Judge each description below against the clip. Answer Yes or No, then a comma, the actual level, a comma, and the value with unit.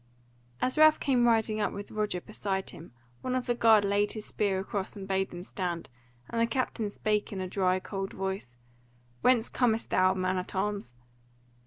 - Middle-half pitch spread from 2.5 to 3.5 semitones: Yes, average, 2.9 semitones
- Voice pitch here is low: No, high, 205 Hz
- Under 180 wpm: No, average, 185 wpm